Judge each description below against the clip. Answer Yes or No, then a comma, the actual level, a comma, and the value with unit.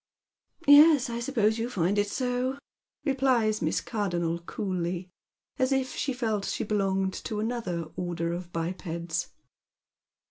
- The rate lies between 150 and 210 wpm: No, average, 140 wpm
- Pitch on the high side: Yes, high, 210 Hz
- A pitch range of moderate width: No, wide, 5.9 semitones